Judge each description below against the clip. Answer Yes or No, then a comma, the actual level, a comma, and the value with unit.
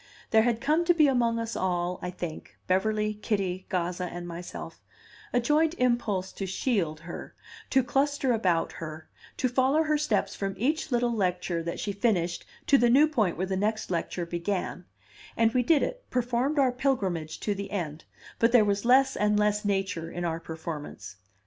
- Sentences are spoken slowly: No, average, 180 wpm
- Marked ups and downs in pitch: Yes, wide, 5.8 semitones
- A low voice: No, high, 210 Hz